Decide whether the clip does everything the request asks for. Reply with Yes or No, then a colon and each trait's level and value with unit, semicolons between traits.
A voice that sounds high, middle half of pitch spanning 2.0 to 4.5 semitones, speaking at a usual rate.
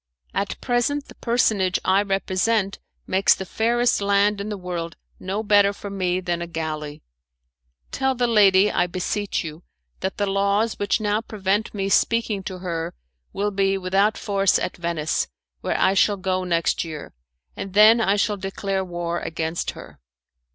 Yes: high, 195 Hz; narrow, 2.4 semitones; average, 165 wpm